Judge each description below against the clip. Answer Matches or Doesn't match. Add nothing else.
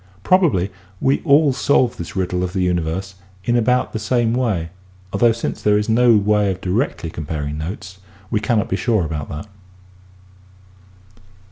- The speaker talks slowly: Doesn't match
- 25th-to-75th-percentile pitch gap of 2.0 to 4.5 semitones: Doesn't match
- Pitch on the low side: Matches